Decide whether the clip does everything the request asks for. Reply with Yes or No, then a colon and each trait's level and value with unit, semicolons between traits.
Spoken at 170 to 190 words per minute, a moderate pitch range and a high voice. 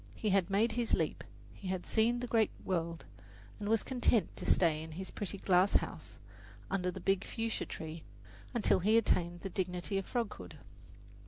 Yes: average, 175 wpm; average, 3.8 semitones; high, 195 Hz